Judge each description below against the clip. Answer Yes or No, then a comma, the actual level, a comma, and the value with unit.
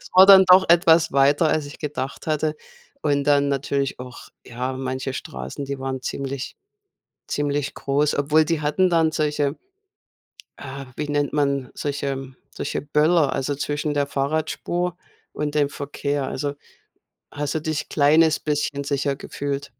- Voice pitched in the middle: Yes, medium, 145 Hz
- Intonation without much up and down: Yes, narrow, 1.7 semitones